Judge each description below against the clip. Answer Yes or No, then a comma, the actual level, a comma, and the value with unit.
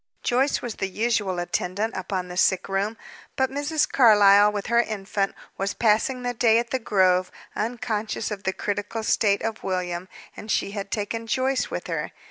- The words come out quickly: No, average, 175 wpm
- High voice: Yes, high, 210 Hz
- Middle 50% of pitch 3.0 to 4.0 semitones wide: Yes, average, 3.3 semitones